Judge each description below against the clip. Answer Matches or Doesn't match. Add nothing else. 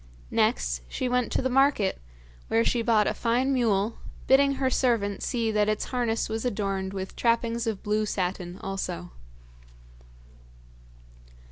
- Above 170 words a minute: Doesn't match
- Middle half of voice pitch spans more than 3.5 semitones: Matches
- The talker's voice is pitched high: Matches